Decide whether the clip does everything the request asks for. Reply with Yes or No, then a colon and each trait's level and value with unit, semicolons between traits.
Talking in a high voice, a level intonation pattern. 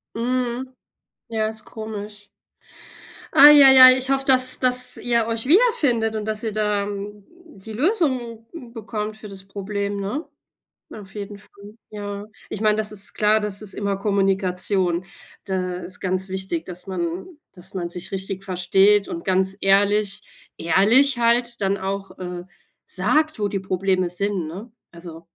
No: high, 205 Hz; average, 3.3 semitones